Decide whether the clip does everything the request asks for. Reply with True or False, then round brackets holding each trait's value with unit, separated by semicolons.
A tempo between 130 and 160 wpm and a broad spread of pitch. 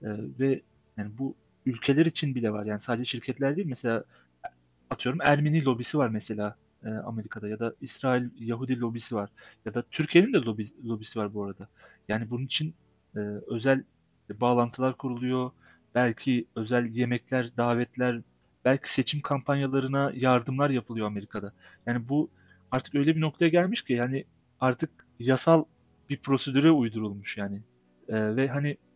False (135 wpm; 3.8 semitones)